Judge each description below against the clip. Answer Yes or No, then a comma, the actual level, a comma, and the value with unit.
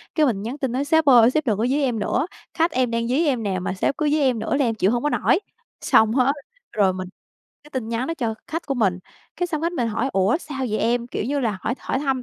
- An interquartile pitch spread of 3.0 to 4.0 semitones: No, average, 4.4 semitones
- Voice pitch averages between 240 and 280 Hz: Yes, very high, 250 Hz